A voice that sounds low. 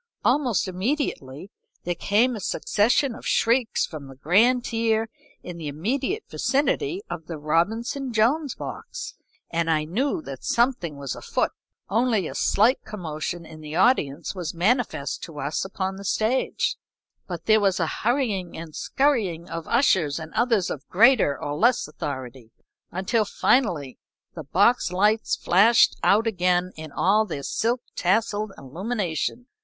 No: high, 195 Hz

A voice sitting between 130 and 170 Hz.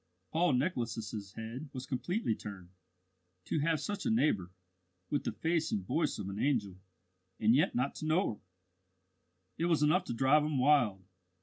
Yes: low, 135 Hz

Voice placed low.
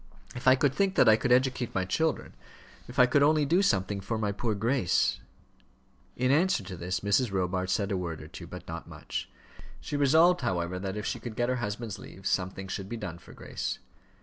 Yes: low, 110 Hz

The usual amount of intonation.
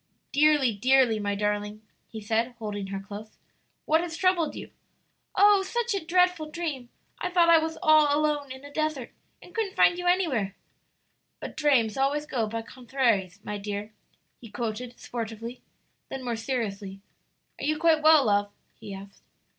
No: wide, 6.6 semitones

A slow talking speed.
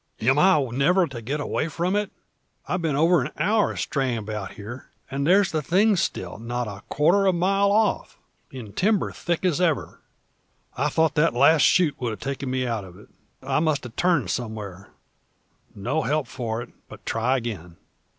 No: average, 190 wpm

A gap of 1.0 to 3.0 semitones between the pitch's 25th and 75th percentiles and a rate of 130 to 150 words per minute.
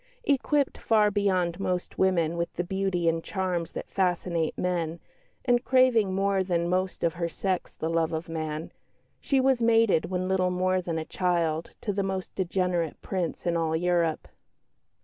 No: narrow, 2.5 semitones; average, 170 wpm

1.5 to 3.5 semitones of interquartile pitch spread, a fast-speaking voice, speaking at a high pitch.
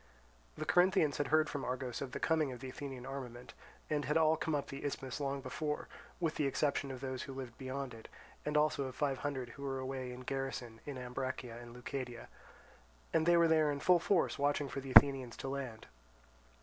No: narrow, 2.4 semitones; fast, 215 wpm; low, 135 Hz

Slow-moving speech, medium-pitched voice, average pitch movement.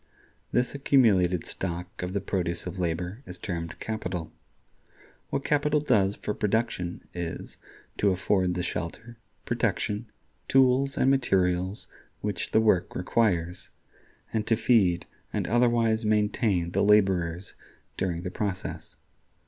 No: slow, 125 wpm; low, 100 Hz; average, 4.2 semitones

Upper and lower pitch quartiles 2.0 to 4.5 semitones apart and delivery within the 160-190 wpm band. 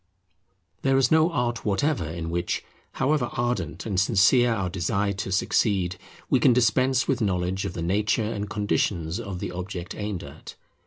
No: average, 5.0 semitones; average, 165 wpm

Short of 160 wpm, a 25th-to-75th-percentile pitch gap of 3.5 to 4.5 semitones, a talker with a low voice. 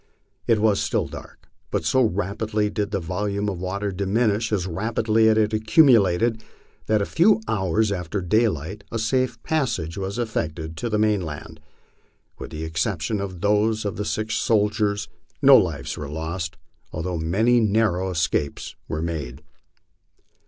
Yes: average, 150 wpm; average, 3.9 semitones; low, 105 Hz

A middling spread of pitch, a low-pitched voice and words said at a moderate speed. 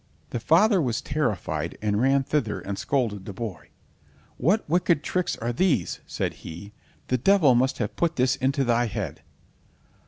No: wide, 6.1 semitones; low, 125 Hz; average, 160 wpm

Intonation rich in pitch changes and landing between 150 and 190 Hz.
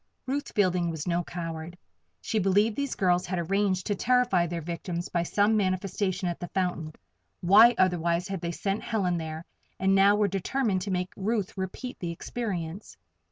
No: average, 2.9 semitones; medium, 185 Hz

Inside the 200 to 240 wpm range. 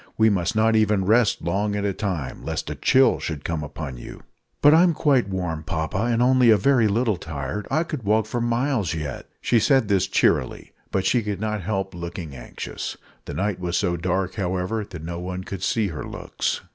Yes: fast, 205 wpm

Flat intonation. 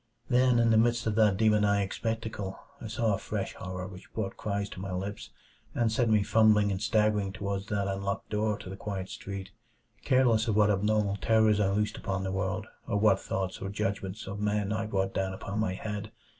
Yes: narrow, 2.0 semitones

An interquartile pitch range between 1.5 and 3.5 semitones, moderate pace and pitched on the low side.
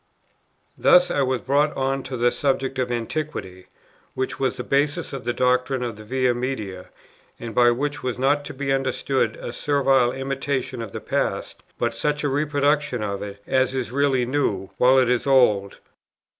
Yes: narrow, 2.5 semitones; average, 180 wpm; low, 130 Hz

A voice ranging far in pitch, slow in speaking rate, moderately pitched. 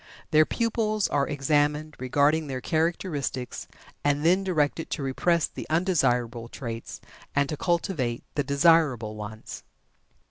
No: average, 4.4 semitones; slow, 120 wpm; medium, 145 Hz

